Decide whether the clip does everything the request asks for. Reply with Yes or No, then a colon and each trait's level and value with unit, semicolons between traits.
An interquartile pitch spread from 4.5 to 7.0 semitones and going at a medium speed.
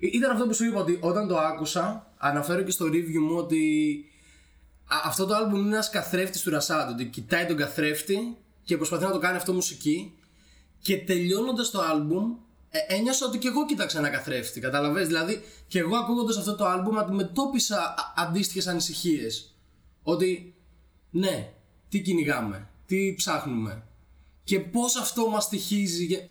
Yes: wide, 5.4 semitones; average, 155 wpm